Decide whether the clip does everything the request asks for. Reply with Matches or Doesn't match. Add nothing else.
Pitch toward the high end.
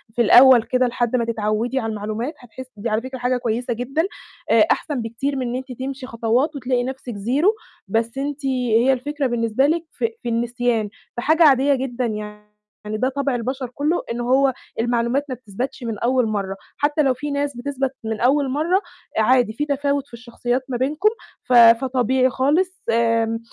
Matches